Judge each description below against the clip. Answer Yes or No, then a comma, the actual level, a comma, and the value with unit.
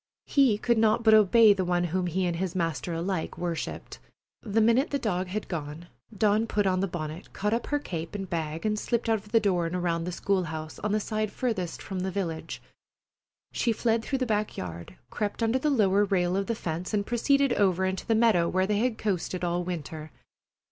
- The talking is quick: Yes, fast, 215 wpm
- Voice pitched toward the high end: Yes, high, 195 Hz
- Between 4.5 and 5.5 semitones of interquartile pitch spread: No, average, 4.0 semitones